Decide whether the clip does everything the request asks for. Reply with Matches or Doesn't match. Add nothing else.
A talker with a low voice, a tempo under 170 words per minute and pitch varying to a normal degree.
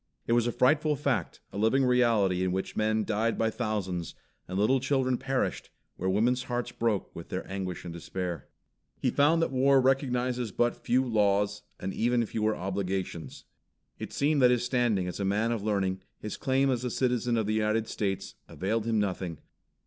Doesn't match